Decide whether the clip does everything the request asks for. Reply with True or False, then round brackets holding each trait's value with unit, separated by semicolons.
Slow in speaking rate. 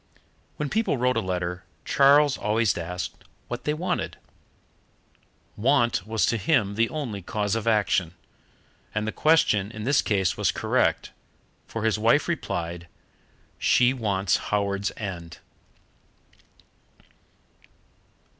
True (115 wpm)